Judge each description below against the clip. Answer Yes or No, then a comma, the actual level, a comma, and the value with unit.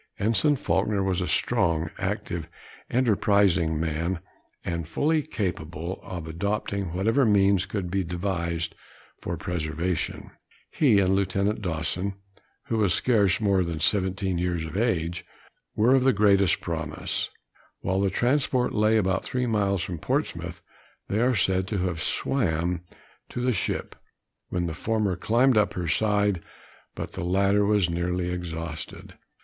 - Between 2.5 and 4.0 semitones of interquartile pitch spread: Yes, average, 3.5 semitones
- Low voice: Yes, very low, 95 Hz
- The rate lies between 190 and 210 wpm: No, average, 145 wpm